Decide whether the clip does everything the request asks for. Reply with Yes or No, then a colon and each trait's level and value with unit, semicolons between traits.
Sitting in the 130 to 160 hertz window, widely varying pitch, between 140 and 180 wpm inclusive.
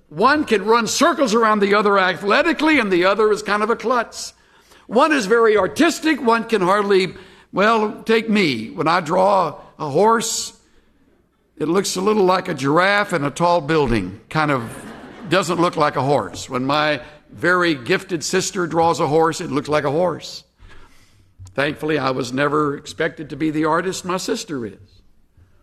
No: medium, 180 Hz; wide, 6.4 semitones; average, 175 wpm